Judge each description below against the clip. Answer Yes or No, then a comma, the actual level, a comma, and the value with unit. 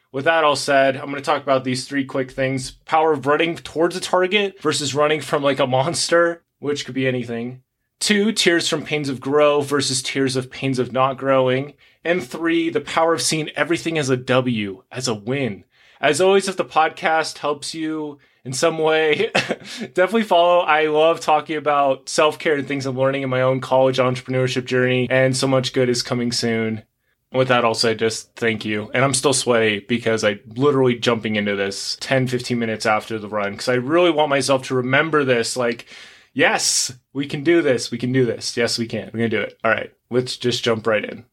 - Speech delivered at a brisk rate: Yes, fast, 210 wpm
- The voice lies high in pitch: No, low, 135 Hz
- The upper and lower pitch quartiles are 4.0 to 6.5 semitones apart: No, average, 3.6 semitones